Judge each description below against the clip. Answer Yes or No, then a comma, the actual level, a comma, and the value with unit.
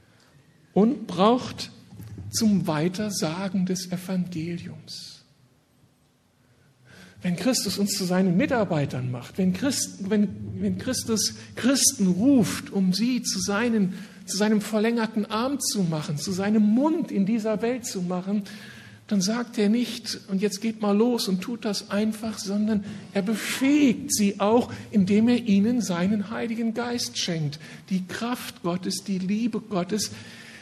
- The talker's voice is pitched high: Yes, high, 205 Hz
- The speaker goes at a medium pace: Yes, average, 135 wpm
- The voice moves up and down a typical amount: Yes, average, 3.5 semitones